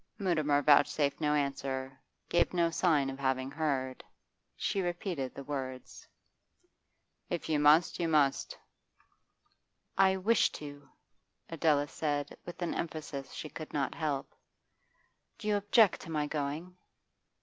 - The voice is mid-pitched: Yes, medium, 150 Hz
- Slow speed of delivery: Yes, slow, 125 wpm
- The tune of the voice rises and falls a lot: No, average, 3.5 semitones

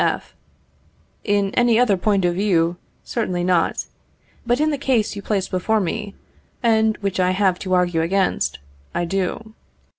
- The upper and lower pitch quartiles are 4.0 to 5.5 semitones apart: No, average, 3.3 semitones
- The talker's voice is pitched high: Yes, high, 195 Hz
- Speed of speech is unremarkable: Yes, average, 155 wpm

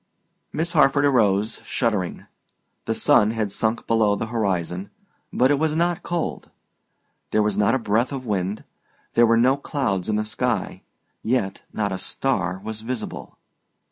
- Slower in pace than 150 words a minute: No, average, 155 wpm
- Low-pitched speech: Yes, low, 110 Hz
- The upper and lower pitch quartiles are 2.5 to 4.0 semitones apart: No, average, 4.4 semitones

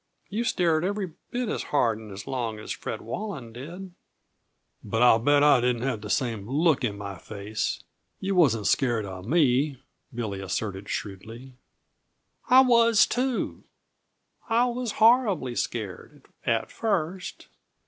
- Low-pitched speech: Yes, low, 130 Hz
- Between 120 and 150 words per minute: Yes, average, 140 wpm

